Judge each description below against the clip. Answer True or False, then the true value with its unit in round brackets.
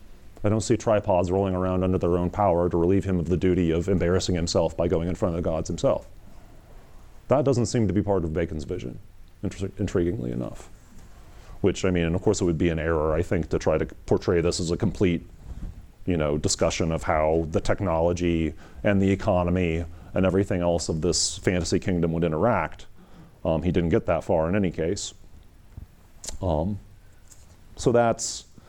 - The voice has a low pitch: True (90 Hz)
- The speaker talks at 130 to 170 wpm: False (190 wpm)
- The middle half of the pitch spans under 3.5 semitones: True (2.5 semitones)